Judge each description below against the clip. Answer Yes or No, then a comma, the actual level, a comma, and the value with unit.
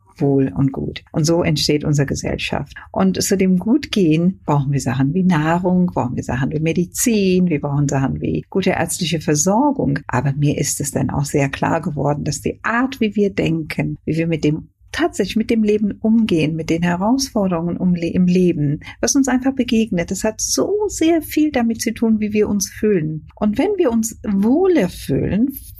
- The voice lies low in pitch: No, medium, 180 Hz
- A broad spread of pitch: Yes, wide, 6.7 semitones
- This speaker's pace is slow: No, fast, 190 wpm